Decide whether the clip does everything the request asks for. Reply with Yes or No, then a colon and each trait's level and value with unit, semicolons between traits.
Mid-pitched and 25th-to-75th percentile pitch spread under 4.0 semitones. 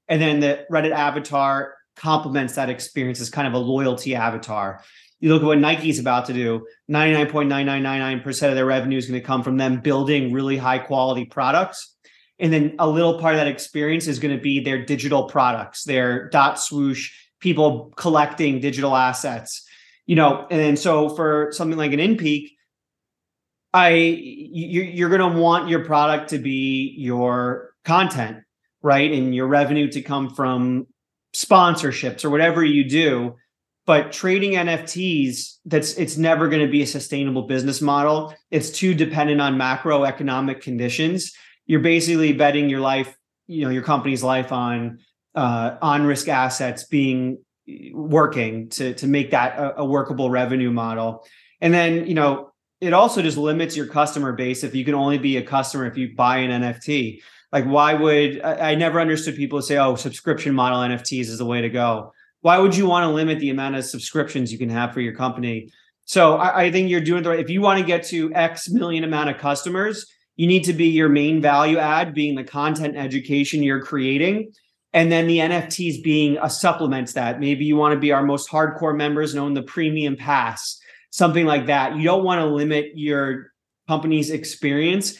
Yes: medium, 145 Hz; average, 3.2 semitones